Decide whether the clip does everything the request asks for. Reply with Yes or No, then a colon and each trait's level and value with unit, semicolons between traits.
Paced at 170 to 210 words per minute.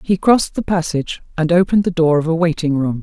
No: fast, 240 wpm